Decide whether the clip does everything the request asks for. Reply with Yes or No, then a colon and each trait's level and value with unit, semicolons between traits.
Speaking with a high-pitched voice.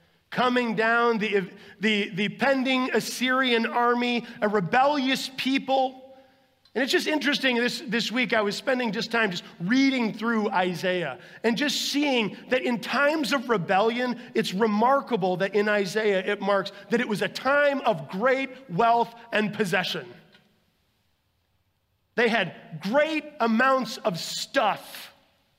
Yes: high, 230 Hz